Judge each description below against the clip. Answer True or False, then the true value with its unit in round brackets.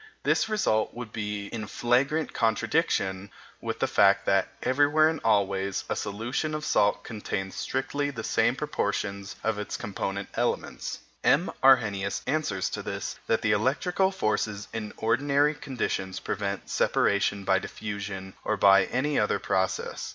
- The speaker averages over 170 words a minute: False (145 wpm)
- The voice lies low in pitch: True (110 Hz)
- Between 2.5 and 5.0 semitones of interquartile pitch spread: False (5.5 semitones)